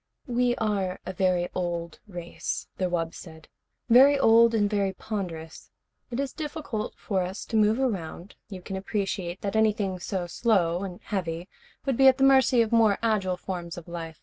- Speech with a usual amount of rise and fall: Yes, average, 4.4 semitones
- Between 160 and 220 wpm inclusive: Yes, average, 175 wpm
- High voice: Yes, high, 195 Hz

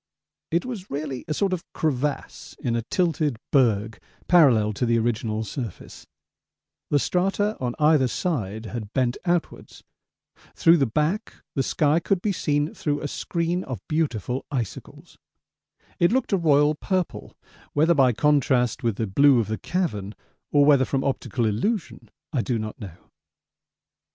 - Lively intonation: Yes, wide, 6.0 semitones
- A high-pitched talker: No, medium, 140 Hz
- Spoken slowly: No, average, 150 wpm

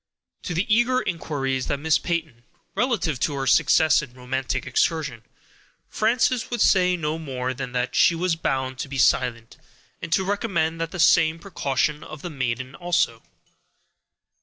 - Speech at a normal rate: Yes, average, 160 wpm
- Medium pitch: Yes, medium, 155 Hz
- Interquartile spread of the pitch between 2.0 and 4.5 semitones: No, average, 5.1 semitones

